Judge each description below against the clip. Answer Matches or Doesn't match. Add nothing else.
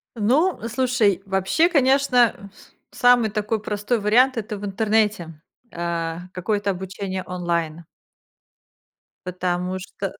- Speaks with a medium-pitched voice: Doesn't match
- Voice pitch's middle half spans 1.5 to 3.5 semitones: Doesn't match